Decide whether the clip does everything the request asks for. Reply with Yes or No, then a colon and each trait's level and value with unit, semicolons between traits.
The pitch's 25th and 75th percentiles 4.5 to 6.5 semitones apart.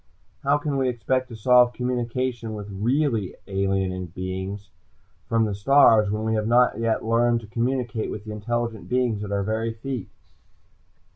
No: average, 3.2 semitones